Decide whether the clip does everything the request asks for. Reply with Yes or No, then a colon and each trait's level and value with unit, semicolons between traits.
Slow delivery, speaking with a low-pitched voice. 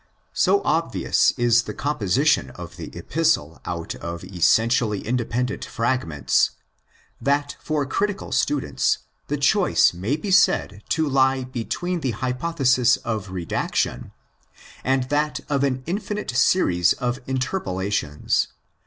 Yes: slow, 120 wpm; low, 130 Hz